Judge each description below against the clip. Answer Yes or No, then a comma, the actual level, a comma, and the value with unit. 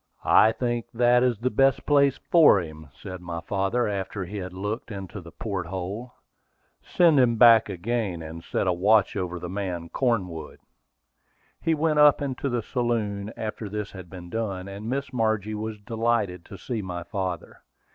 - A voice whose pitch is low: Yes, low, 105 Hz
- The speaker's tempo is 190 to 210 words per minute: No, average, 175 wpm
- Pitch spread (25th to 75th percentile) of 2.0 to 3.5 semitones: No, average, 4.4 semitones